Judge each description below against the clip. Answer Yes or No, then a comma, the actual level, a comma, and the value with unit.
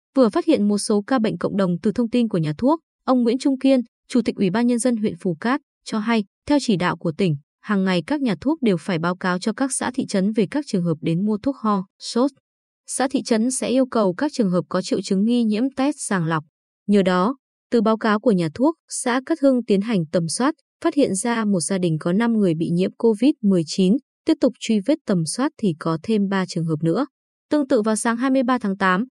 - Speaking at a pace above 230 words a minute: Yes, fast, 250 wpm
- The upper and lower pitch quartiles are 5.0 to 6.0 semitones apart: Yes, wide, 5.4 semitones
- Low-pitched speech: No, high, 225 Hz